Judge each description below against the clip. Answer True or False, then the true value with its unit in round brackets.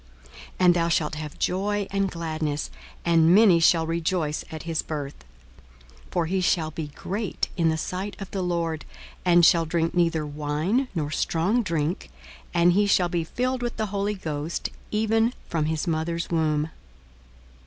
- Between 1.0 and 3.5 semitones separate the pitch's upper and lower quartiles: True (3.2 semitones)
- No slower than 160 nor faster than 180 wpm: True (165 wpm)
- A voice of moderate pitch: True (170 Hz)